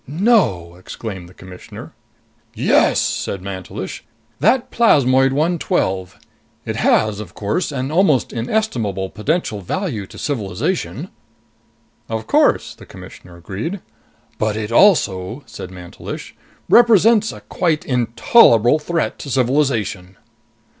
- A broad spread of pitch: Yes, wide, 8.9 semitones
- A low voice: Yes, low, 120 Hz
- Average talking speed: No, slow, 110 wpm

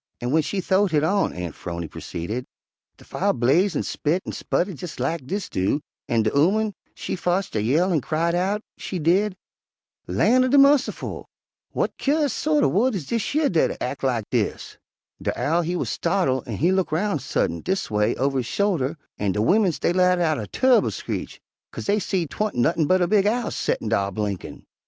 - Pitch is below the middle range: No, medium, 170 Hz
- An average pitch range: No, wide, 7.6 semitones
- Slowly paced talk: No, fast, 205 wpm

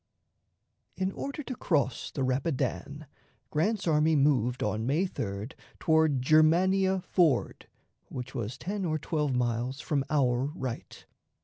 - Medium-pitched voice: Yes, medium, 150 Hz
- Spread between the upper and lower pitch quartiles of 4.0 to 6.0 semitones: Yes, average, 4.8 semitones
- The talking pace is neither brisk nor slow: No, slow, 125 wpm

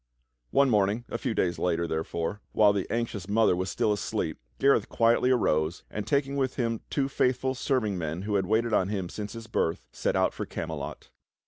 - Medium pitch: No, low, 105 Hz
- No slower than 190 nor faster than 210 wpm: Yes, average, 200 wpm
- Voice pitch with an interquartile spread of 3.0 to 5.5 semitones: Yes, average, 4.7 semitones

